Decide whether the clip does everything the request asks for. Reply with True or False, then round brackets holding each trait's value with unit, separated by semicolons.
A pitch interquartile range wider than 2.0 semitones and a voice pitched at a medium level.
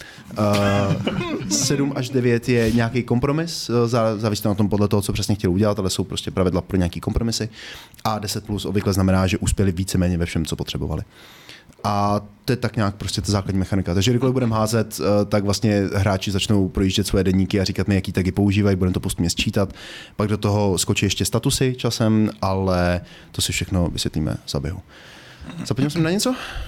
False (2.7 semitones; 105 Hz)